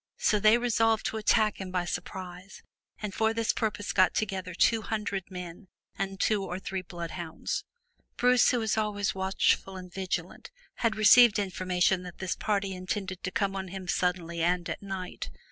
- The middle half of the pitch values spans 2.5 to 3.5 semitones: Yes, average, 2.8 semitones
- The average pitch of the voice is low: No, high, 195 Hz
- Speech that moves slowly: No, average, 175 wpm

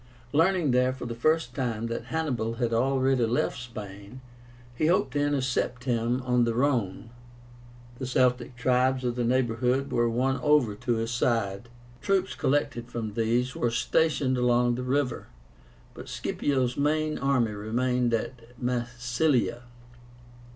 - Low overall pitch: Yes, low, 125 Hz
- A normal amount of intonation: No, narrow, 2.1 semitones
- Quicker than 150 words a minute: No, average, 140 wpm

